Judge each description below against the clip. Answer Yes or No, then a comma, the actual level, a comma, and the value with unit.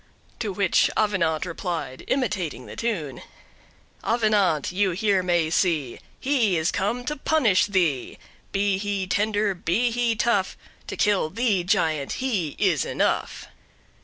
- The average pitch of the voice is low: No, high, 195 Hz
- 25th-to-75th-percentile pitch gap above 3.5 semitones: Yes, average, 4.3 semitones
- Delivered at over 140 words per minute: No, slow, 135 wpm